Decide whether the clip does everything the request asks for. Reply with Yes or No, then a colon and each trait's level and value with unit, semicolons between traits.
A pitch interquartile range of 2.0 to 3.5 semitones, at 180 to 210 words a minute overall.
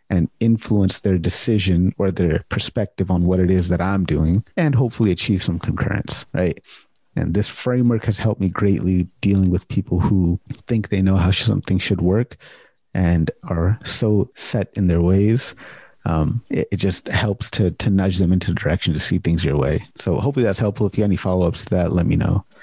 Yes: average, 3.0 semitones; average, 200 wpm